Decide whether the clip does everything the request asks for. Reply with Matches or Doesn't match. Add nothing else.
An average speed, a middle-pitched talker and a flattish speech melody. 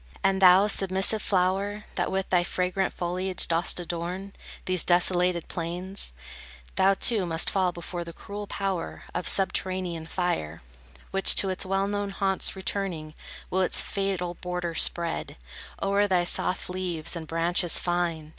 Matches